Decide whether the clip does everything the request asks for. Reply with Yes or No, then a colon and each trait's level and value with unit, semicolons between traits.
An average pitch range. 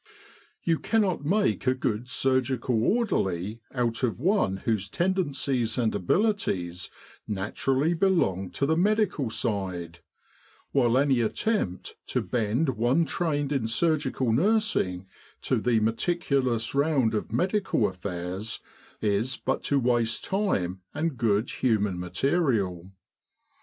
No: wide, 7.2 semitones